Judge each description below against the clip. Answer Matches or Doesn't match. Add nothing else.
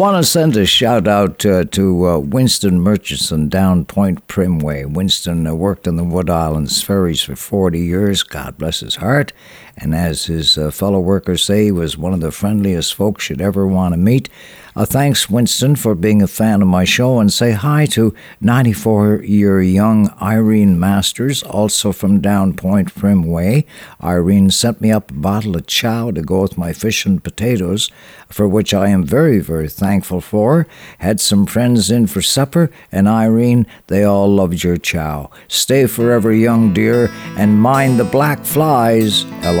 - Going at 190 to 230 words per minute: Doesn't match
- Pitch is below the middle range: Matches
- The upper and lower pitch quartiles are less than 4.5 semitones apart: Matches